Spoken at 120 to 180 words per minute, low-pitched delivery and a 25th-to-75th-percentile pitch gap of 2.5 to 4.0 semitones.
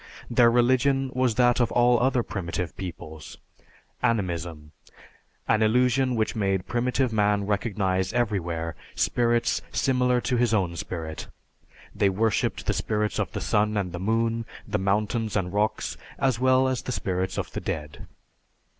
No: average, 145 wpm; low, 110 Hz; average, 4.5 semitones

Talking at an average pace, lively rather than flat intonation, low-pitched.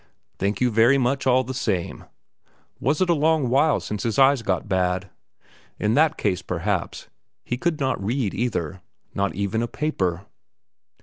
Yes: average, 150 wpm; wide, 5.9 semitones; low, 115 Hz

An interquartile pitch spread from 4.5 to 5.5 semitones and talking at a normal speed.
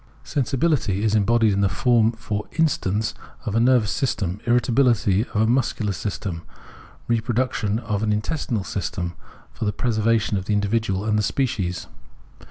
No: average, 2.7 semitones; average, 160 wpm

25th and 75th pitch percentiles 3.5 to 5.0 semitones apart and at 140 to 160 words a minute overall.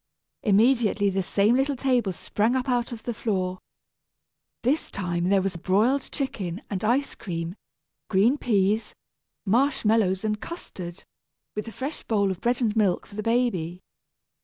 Yes: average, 4.3 semitones; average, 155 wpm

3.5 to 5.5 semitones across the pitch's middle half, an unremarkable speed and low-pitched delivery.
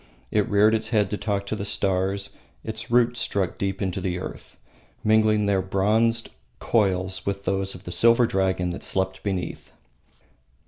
No: narrow, 2.4 semitones; average, 165 wpm; low, 100 Hz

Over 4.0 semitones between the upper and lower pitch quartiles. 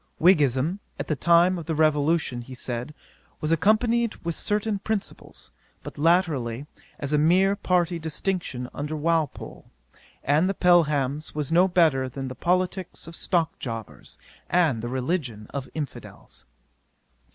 Yes: average, 4.6 semitones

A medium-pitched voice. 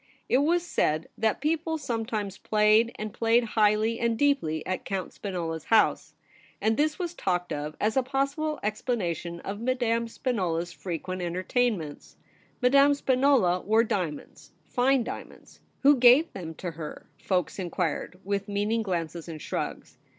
No: high, 215 Hz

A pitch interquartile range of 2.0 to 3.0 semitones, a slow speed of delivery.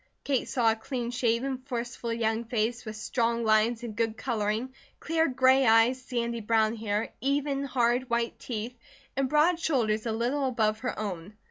No: average, 2.7 semitones; average, 165 wpm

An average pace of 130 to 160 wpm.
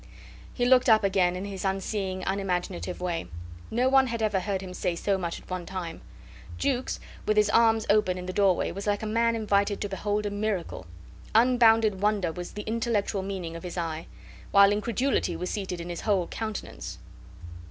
No: average, 185 wpm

